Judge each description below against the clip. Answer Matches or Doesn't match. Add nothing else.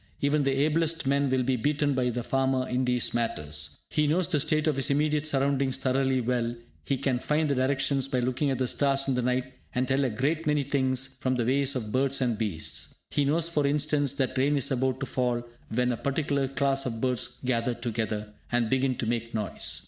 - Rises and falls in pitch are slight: Matches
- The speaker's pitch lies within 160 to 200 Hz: Doesn't match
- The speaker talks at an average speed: Doesn't match